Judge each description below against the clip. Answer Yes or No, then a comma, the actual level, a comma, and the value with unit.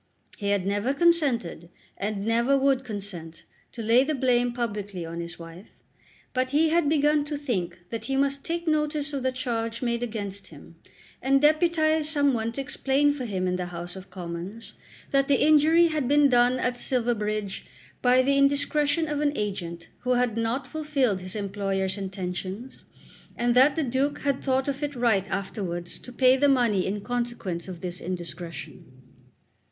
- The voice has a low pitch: No, high, 240 Hz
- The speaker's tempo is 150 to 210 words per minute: Yes, average, 170 wpm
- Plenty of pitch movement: Yes, wide, 6.4 semitones